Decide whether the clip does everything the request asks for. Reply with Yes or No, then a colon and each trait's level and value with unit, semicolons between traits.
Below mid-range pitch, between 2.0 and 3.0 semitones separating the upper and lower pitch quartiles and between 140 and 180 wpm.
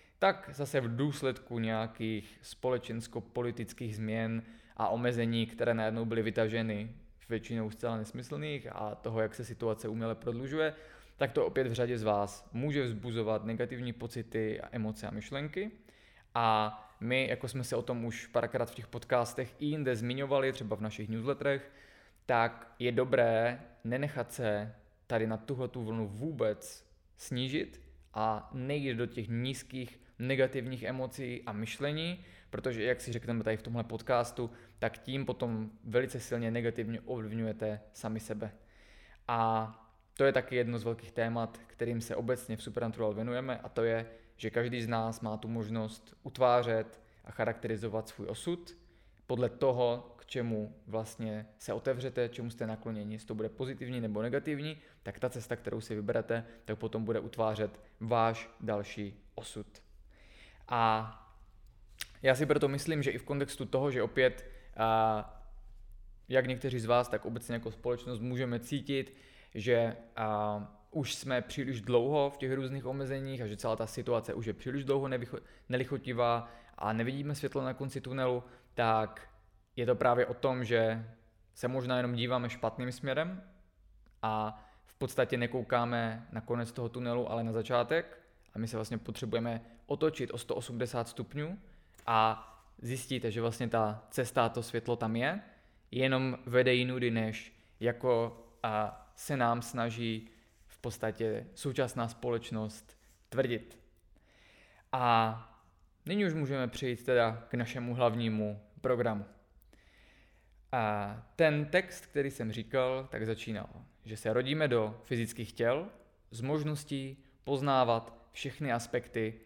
Yes: low, 115 Hz; narrow, 2.4 semitones; average, 145 wpm